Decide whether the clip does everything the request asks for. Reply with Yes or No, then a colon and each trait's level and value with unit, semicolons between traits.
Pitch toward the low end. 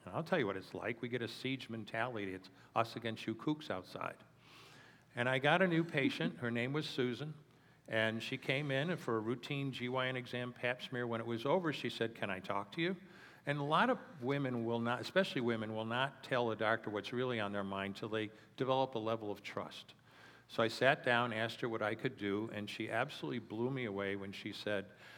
Yes: low, 120 Hz